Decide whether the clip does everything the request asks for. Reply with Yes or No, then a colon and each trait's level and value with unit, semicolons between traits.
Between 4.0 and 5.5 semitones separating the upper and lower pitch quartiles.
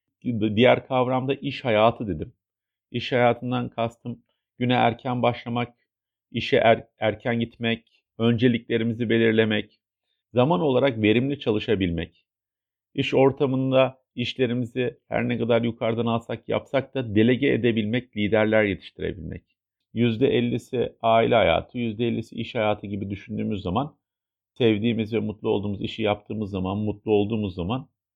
No: narrow, 2.6 semitones